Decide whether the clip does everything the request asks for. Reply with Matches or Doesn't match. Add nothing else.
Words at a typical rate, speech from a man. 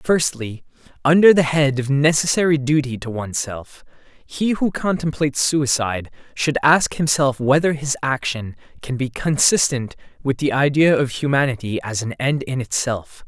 Matches